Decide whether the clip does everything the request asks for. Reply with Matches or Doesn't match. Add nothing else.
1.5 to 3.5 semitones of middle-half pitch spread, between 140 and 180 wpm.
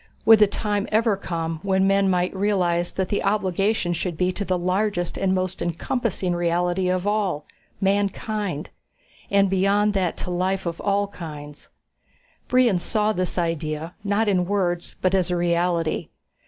Matches